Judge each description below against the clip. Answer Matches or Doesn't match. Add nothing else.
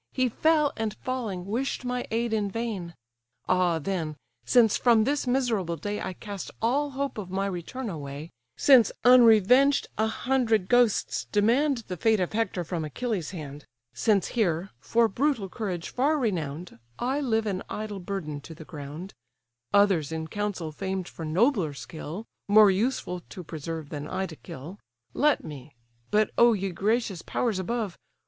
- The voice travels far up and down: Matches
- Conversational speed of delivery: Matches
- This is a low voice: Doesn't match